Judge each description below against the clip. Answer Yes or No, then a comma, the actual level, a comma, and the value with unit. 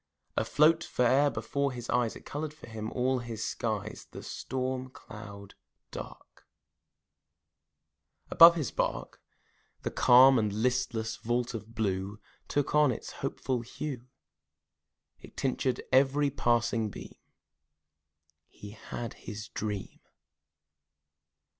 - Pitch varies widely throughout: No, average, 3.3 semitones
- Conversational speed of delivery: No, slow, 110 wpm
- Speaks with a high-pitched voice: No, low, 120 Hz